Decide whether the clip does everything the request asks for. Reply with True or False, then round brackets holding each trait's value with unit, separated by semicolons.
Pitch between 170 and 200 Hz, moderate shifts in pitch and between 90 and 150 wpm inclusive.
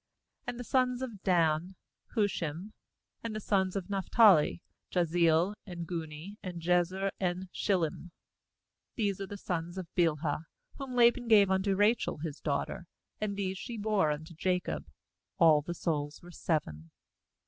True (185 Hz; 3.7 semitones; 145 wpm)